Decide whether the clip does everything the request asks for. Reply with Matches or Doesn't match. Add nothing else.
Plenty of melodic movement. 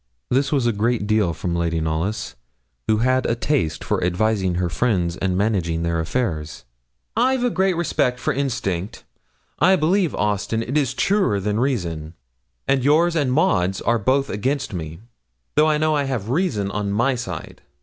Matches